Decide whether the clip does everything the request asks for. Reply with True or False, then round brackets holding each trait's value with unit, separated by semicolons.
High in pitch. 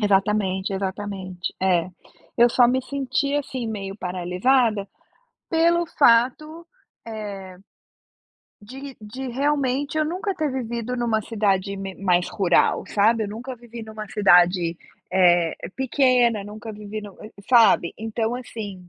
True (220 Hz)